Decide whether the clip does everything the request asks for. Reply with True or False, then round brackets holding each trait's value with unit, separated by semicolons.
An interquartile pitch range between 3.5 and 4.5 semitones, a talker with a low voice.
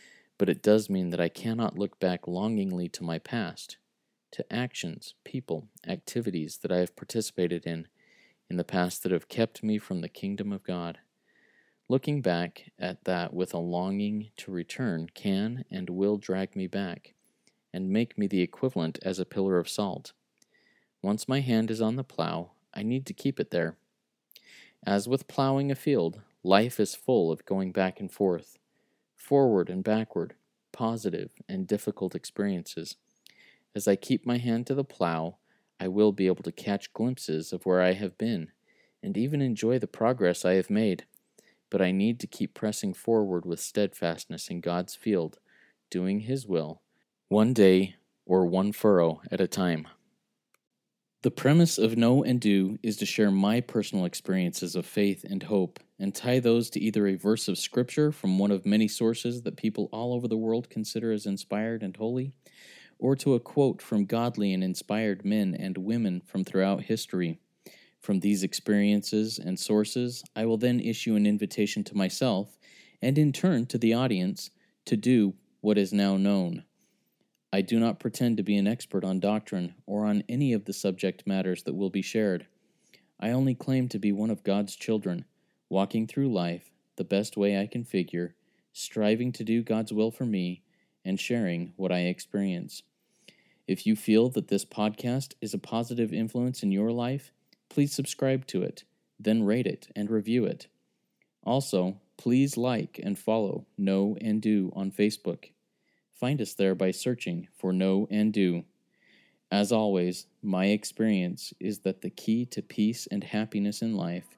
True (3.8 semitones; 105 Hz)